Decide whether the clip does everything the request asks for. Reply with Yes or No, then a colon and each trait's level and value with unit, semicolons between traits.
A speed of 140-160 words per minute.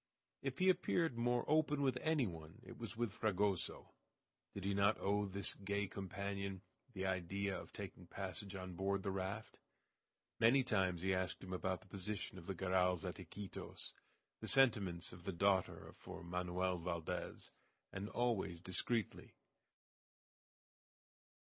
Yes: average, 150 wpm